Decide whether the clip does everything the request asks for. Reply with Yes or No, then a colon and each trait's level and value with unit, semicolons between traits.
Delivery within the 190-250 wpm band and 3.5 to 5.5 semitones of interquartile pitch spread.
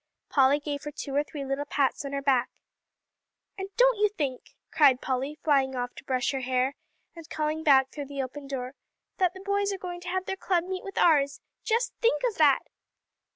Yes: fast, 205 wpm; average, 5.2 semitones